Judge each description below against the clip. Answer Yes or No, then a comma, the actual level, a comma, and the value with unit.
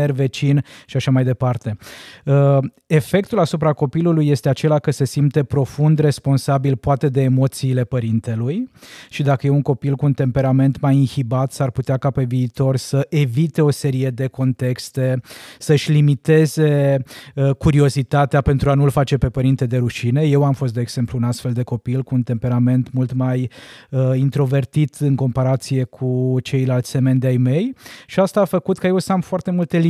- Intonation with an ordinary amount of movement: No, narrow, 2.3 semitones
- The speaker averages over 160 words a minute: Yes, fast, 170 wpm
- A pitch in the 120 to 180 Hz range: Yes, low, 135 Hz